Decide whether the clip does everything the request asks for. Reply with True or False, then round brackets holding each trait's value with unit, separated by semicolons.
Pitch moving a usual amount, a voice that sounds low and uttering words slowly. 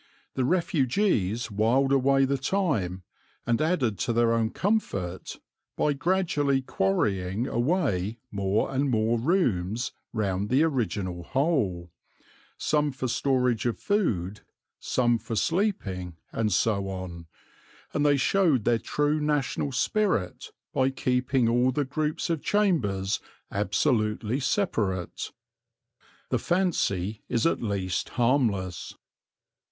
False (6.4 semitones; 120 Hz; 115 wpm)